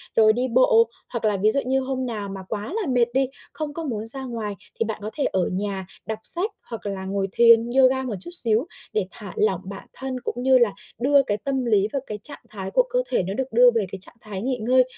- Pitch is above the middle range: Yes, high, 230 Hz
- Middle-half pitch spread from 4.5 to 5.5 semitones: No, average, 4.0 semitones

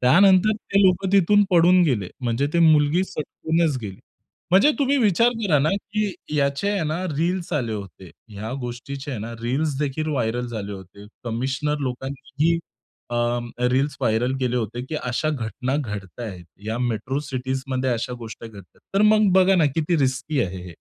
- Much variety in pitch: Yes, wide, 6.1 semitones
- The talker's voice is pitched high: No, low, 135 Hz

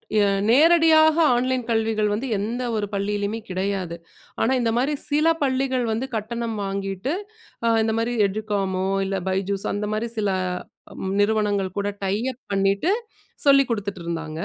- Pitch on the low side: No, high, 215 Hz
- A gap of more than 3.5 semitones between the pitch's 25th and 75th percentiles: Yes, average, 4.3 semitones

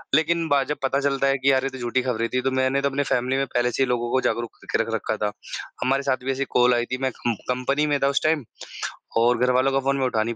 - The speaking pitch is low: Yes, low, 130 Hz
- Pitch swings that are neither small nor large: No, narrow, 1.8 semitones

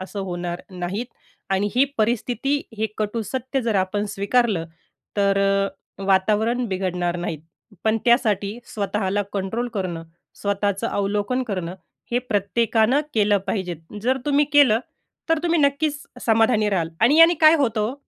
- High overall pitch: Yes, high, 215 Hz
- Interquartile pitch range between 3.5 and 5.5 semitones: Yes, average, 4.2 semitones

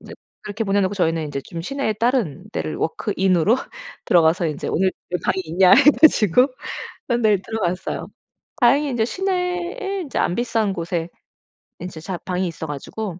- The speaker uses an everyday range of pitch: No, wide, 5.9 semitones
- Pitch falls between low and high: No, high, 195 Hz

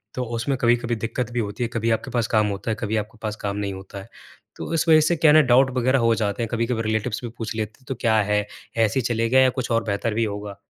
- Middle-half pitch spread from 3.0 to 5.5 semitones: No, narrow, 2.5 semitones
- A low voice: Yes, low, 115 Hz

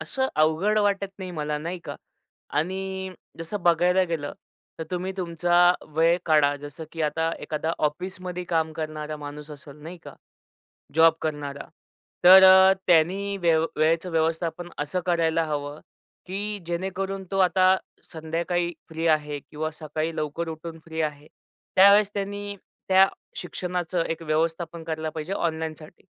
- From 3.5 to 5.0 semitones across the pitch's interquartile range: No, average, 2.9 semitones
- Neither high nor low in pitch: Yes, medium, 165 Hz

